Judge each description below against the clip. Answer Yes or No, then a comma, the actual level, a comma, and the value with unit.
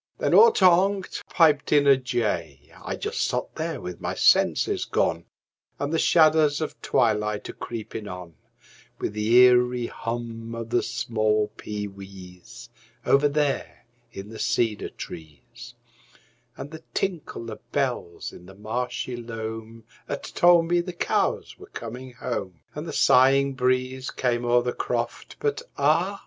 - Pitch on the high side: No, low, 120 Hz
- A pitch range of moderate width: Yes, average, 4.7 semitones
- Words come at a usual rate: Yes, average, 150 wpm